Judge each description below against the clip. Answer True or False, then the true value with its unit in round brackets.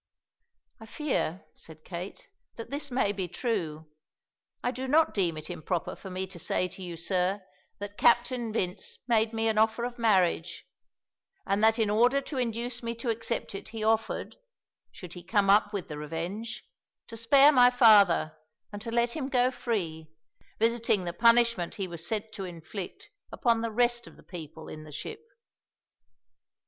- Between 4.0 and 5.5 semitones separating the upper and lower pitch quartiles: True (4.8 semitones)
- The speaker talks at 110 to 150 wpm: False (175 wpm)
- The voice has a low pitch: False (215 Hz)